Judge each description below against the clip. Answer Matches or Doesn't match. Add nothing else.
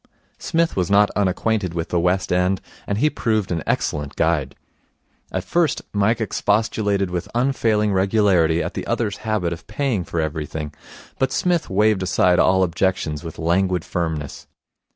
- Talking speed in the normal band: Matches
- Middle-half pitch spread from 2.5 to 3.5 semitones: Doesn't match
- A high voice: Doesn't match